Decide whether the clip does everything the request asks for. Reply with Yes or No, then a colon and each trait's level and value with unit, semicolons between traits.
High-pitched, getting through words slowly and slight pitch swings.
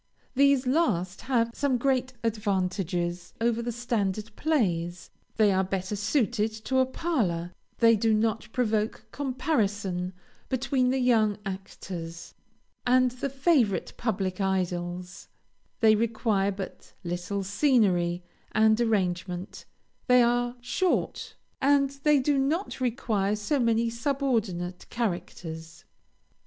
No: high, 220 Hz; slow, 115 wpm; average, 5.2 semitones